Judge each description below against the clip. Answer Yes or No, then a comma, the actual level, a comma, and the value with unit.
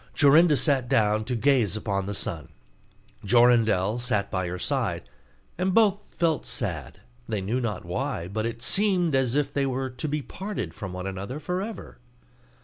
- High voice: No, low, 125 Hz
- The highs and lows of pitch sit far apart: Yes, wide, 6.2 semitones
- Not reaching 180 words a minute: Yes, average, 170 wpm